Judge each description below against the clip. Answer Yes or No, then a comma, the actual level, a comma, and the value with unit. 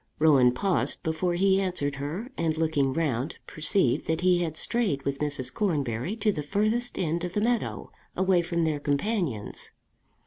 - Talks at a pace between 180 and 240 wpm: No, average, 165 wpm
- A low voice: No, medium, 165 Hz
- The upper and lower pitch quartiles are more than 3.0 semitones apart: Yes, average, 5.0 semitones